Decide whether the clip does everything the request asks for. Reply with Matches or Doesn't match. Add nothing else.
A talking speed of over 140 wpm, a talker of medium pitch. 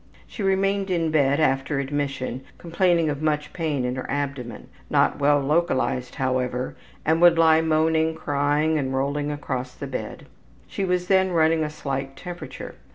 Matches